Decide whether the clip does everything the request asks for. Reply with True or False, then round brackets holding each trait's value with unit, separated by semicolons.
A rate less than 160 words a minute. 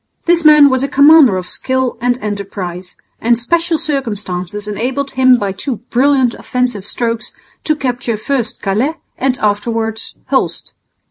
True (140 wpm)